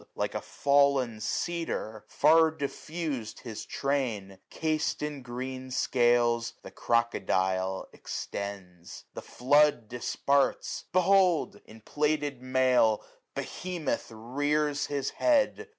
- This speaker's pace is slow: Yes, slow, 100 wpm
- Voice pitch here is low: Yes, low, 130 Hz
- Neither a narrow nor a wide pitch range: Yes, average, 4.4 semitones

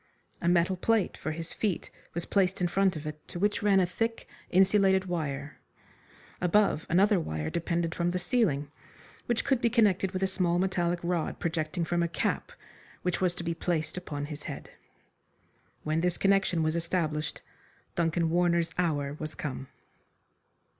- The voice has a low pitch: No, medium, 175 Hz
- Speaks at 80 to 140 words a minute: No, average, 165 wpm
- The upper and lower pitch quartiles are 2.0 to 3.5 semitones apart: Yes, average, 2.9 semitones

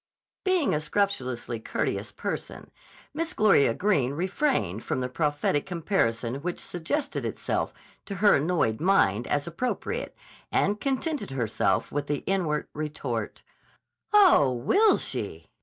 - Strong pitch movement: Yes, wide, 8.3 semitones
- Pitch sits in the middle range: Yes, medium, 160 Hz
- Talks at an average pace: No, slow, 125 wpm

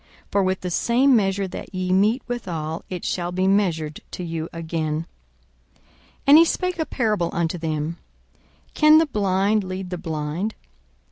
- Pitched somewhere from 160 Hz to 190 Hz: Yes, medium, 185 Hz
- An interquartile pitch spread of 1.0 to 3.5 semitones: No, average, 4.3 semitones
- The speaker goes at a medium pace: Yes, average, 160 wpm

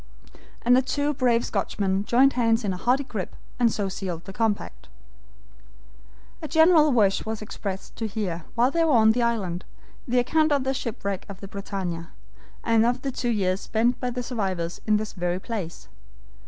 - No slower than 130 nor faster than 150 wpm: No, average, 180 wpm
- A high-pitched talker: Yes, high, 220 Hz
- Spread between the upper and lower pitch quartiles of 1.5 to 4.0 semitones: No, average, 4.4 semitones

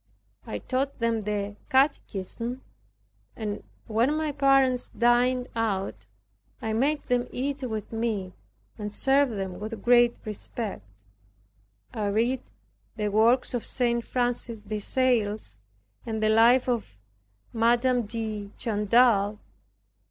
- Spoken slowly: Yes, slow, 115 wpm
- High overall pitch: Yes, high, 230 Hz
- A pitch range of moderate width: Yes, average, 3.0 semitones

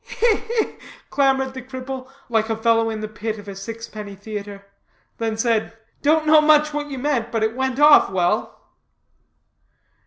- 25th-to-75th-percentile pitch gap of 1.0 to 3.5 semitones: No, average, 4.3 semitones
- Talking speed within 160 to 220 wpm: Yes, average, 165 wpm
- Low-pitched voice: No, high, 230 Hz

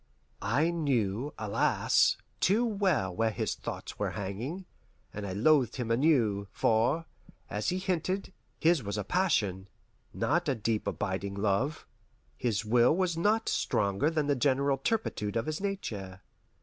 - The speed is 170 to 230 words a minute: No, average, 145 wpm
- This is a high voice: No, low, 125 Hz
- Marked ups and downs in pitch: Yes, wide, 8.2 semitones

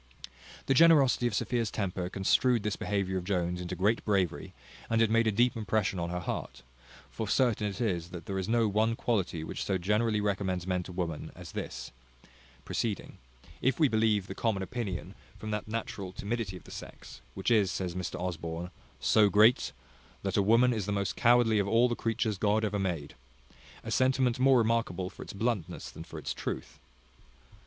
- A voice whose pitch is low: Yes, low, 105 Hz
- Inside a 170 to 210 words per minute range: Yes, average, 190 wpm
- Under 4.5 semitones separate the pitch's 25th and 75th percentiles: Yes, average, 3.7 semitones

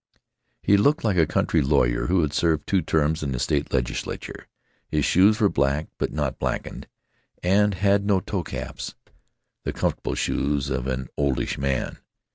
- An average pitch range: No, wide, 5.9 semitones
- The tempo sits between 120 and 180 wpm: Yes, average, 160 wpm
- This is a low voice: Yes, very low, 75 Hz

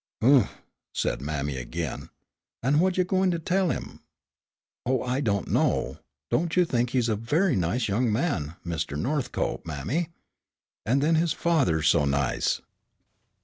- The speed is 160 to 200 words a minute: No, average, 145 wpm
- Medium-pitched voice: No, low, 125 Hz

